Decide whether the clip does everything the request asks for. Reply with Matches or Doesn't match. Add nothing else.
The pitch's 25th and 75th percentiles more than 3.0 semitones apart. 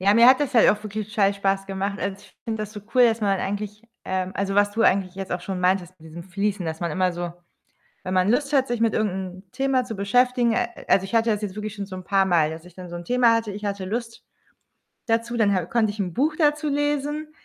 Matches